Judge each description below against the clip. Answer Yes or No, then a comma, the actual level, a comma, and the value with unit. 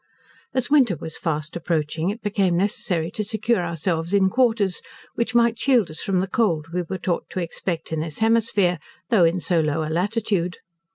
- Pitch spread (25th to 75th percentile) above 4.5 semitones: Yes, average, 4.9 semitones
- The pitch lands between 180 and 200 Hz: Yes, medium, 185 Hz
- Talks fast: No, average, 185 wpm